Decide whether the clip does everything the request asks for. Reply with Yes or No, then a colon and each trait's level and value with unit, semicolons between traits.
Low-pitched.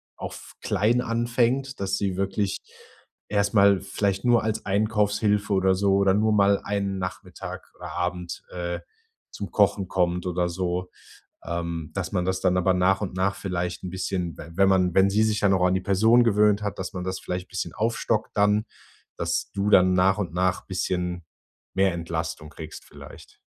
Yes: very low, 95 Hz